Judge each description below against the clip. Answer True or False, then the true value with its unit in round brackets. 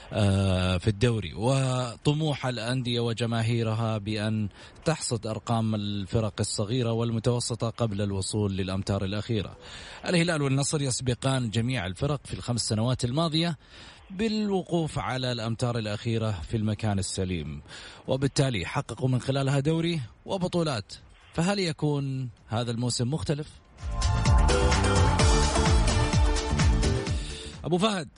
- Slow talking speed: True (95 wpm)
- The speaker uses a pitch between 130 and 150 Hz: False (115 Hz)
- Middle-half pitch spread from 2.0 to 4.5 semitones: False (5.2 semitones)